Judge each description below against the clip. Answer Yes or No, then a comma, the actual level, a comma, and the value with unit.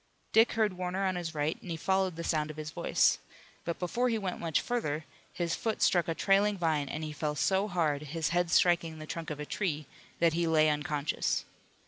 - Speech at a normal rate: No, fast, 215 wpm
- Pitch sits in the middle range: Yes, medium, 170 Hz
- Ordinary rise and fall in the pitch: Yes, average, 3.3 semitones